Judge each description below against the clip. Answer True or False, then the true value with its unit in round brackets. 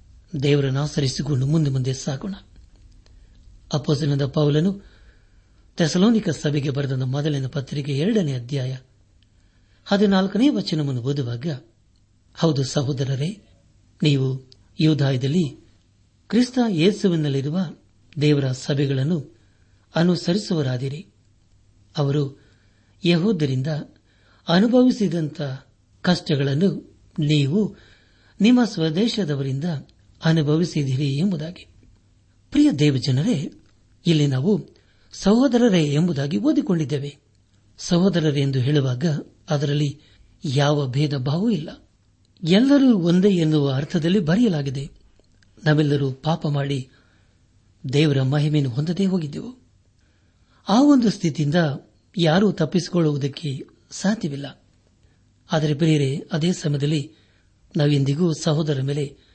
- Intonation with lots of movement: True (7.3 semitones)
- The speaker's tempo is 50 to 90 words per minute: True (75 wpm)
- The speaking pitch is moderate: True (145 Hz)